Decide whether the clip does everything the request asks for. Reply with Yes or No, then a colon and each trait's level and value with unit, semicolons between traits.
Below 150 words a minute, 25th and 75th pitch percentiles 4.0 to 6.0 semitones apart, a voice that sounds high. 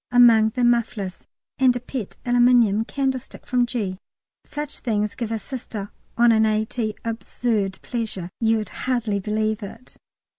No: average, 140 wpm; narrow, 2.4 semitones; high, 225 Hz